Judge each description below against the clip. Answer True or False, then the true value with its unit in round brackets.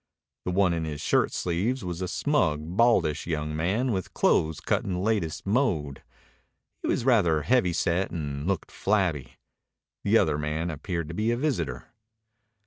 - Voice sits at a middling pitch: False (85 Hz)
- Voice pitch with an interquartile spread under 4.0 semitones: False (5.0 semitones)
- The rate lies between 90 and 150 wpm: False (165 wpm)